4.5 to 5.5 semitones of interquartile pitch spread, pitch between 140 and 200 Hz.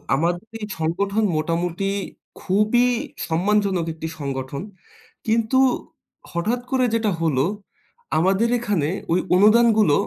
Yes: average, 4.9 semitones; high, 190 Hz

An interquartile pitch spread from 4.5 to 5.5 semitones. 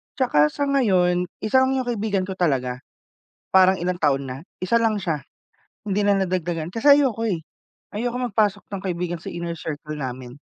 Yes: average, 5.0 semitones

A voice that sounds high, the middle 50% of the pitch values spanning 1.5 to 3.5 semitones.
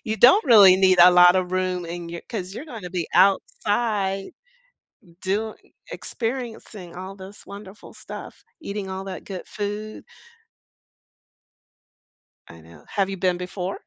Yes: high, 195 Hz; average, 2.8 semitones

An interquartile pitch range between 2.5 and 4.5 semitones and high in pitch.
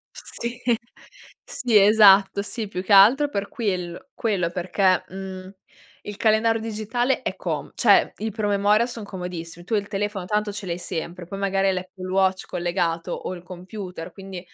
Yes: average, 2.8 semitones; high, 195 Hz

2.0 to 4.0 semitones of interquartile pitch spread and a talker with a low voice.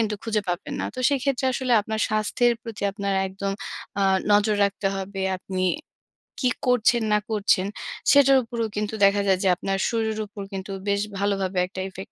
No: average, 2.7 semitones; high, 205 Hz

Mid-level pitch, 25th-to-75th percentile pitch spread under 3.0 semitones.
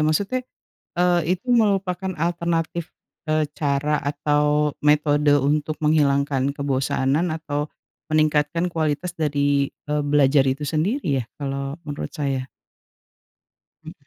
Yes: medium, 150 Hz; narrow, 2.5 semitones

